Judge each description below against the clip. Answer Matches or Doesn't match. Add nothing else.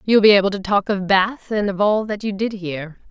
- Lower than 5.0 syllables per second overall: Doesn't match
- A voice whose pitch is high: Matches